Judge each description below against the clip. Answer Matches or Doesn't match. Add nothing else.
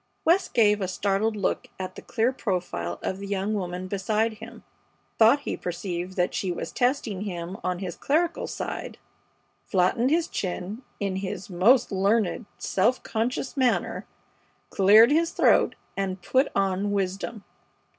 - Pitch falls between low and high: Doesn't match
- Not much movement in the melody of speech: Doesn't match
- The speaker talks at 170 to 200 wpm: Doesn't match